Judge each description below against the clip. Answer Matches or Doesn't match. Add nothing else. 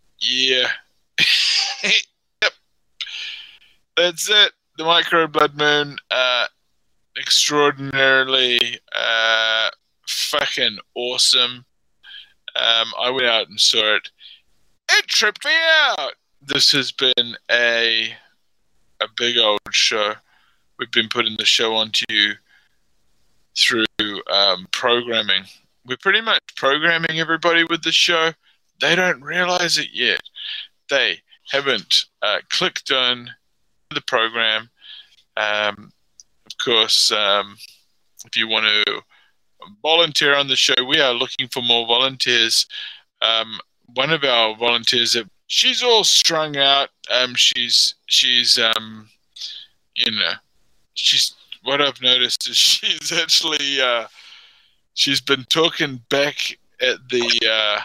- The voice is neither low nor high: Doesn't match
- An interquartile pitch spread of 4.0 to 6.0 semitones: Matches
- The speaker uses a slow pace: Matches